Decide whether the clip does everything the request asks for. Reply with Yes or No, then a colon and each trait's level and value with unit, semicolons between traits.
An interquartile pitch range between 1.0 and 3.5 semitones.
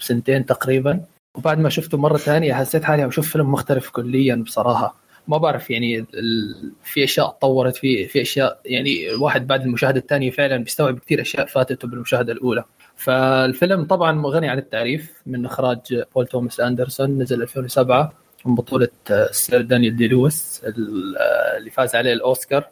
Yes: average, 3.2 semitones